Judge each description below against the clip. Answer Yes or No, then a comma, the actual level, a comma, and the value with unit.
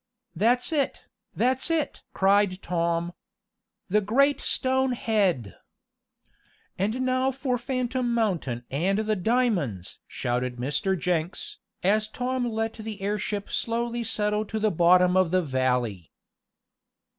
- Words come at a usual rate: No, slow, 120 wpm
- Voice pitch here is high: Yes, high, 210 Hz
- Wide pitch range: Yes, wide, 5.9 semitones